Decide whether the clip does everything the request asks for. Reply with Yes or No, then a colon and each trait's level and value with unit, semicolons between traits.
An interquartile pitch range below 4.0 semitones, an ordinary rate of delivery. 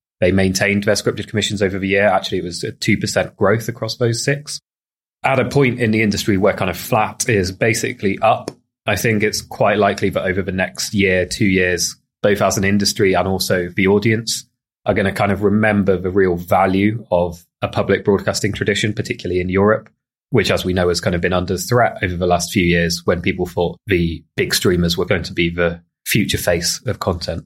No: average, 3.1 semitones; fast, 210 wpm